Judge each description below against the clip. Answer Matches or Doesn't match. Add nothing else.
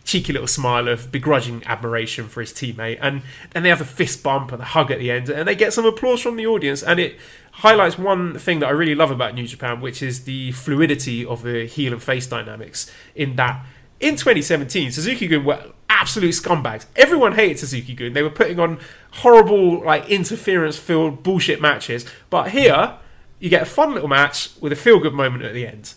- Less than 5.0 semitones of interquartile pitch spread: Doesn't match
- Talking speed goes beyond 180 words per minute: Matches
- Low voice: Doesn't match